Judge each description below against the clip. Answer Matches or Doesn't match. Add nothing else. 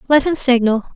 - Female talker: Matches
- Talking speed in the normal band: Matches